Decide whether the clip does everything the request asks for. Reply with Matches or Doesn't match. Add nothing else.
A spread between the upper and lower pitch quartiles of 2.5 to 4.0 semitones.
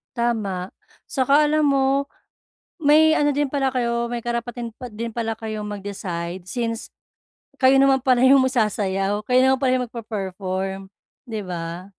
Doesn't match